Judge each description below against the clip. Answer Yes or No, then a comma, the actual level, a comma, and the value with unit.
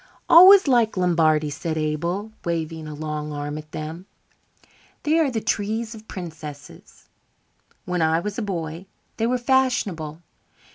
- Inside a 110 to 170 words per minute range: Yes, average, 140 wpm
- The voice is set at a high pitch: No, medium, 170 Hz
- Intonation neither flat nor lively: No, wide, 6.2 semitones